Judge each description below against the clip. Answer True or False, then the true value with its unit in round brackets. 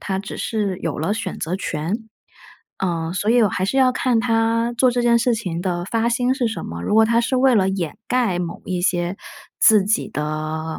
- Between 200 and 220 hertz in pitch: True (205 Hz)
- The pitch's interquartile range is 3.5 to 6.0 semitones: True (5.1 semitones)